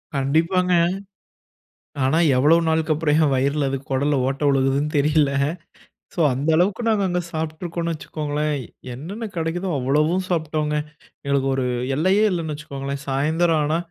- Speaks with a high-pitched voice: No, medium, 155 Hz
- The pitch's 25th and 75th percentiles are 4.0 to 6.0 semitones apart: No, average, 3.1 semitones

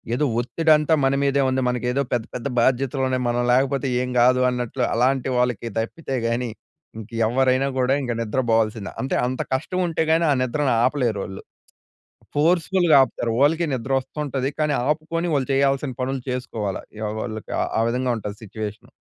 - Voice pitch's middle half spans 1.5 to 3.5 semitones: Yes, average, 2.7 semitones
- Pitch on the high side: No, low, 130 Hz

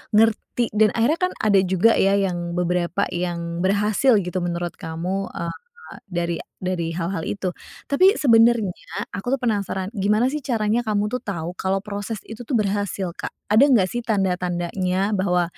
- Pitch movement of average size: Yes, average, 3.8 semitones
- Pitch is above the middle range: Yes, high, 195 Hz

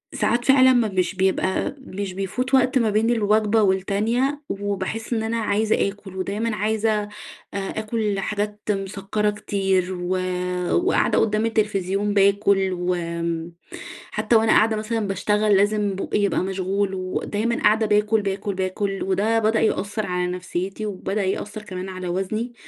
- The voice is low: No, high, 205 Hz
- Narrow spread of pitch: Yes, narrow, 2.3 semitones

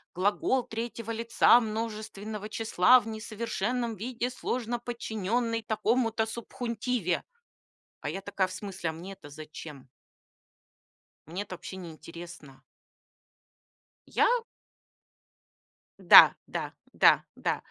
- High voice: Yes, high, 215 Hz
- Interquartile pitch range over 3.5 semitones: Yes, average, 3.9 semitones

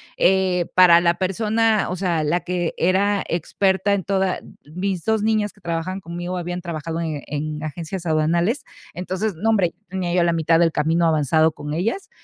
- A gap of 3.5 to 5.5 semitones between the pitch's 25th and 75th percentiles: No, average, 2.7 semitones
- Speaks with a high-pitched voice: No, medium, 175 Hz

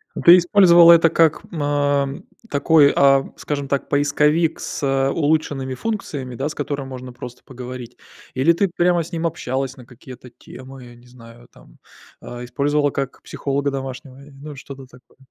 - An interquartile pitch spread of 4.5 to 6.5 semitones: No, average, 3.0 semitones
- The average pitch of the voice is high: No, medium, 140 Hz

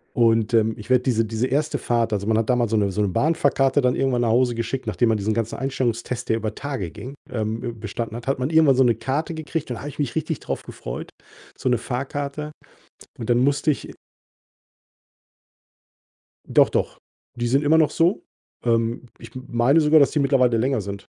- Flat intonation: No, average, 3.5 semitones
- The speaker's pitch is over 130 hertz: No, low, 125 Hz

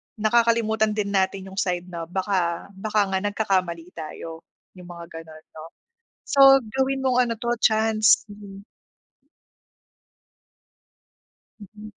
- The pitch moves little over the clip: No, average, 3.7 semitones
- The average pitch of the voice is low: No, high, 200 Hz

